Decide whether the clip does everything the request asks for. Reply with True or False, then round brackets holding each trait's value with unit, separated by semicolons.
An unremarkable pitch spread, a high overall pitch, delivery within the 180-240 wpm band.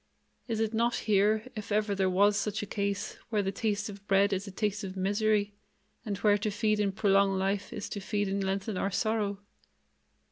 False (1.4 semitones; 205 Hz; 205 wpm)